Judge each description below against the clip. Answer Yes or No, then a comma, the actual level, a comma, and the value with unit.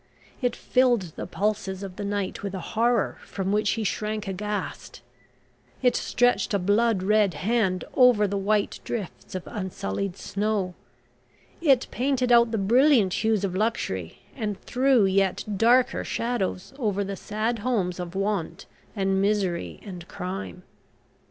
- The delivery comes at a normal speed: Yes, average, 145 wpm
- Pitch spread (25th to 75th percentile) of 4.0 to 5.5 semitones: No, average, 3.3 semitones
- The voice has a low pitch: No, high, 205 Hz